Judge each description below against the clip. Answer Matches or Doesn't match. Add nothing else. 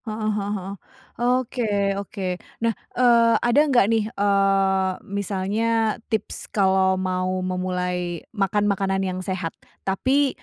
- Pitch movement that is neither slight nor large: Matches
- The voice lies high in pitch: Matches